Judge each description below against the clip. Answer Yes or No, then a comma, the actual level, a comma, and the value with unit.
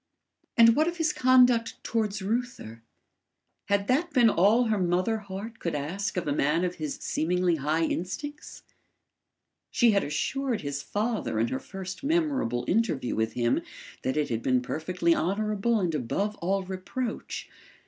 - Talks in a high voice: Yes, high, 195 Hz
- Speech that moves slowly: No, average, 155 wpm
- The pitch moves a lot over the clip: Yes, wide, 6.6 semitones